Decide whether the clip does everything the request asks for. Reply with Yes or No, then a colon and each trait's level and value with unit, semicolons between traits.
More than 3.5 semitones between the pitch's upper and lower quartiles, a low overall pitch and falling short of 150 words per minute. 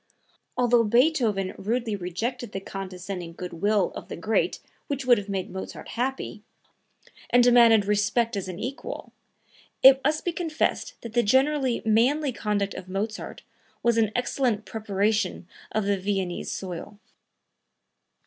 No: average, 4.0 semitones; high, 220 Hz; average, 140 wpm